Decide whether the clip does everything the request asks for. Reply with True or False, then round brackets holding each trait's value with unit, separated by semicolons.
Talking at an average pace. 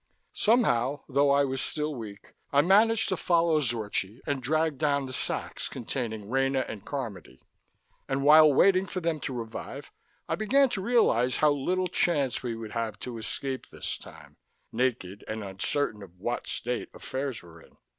True (165 wpm)